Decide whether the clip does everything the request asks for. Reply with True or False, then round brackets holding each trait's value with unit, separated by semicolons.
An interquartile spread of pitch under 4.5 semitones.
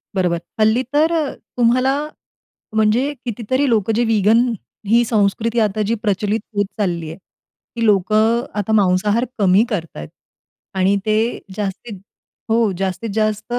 True (2.9 semitones)